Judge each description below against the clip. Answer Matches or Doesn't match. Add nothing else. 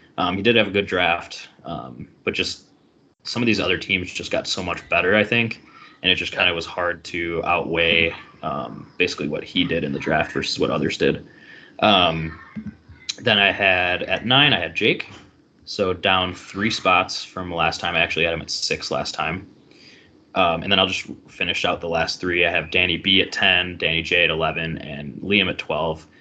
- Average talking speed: Doesn't match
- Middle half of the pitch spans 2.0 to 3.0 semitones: Matches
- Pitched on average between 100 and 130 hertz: Doesn't match